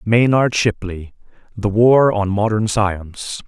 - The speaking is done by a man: Yes, male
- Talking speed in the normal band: No, slow, 120 wpm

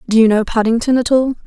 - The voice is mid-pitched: No, high, 235 Hz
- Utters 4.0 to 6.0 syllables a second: No, 6.6 syllables/s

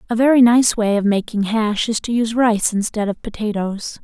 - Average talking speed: No, fast, 210 wpm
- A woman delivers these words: Yes, female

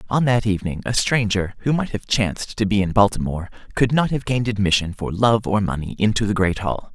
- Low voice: Yes, low, 105 Hz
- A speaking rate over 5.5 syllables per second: Yes, 6.0 syllables/s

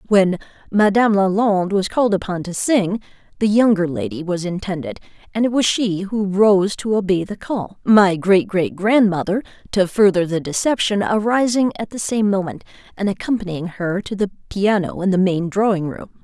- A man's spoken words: No, female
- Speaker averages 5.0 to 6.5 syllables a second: Yes, 5.2 syllables/s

